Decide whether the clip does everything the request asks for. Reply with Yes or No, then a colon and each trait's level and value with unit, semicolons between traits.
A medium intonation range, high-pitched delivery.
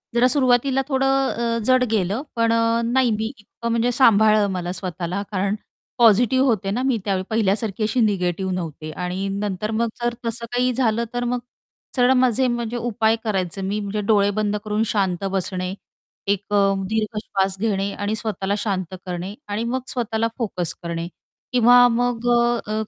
Yes: average, 3.5 semitones; high, 215 Hz